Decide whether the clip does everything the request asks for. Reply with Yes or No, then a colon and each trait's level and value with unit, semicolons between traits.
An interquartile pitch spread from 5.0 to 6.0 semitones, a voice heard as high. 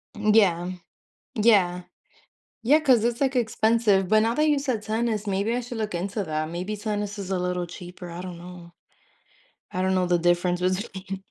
No: average, 3.8 semitones; high, 195 Hz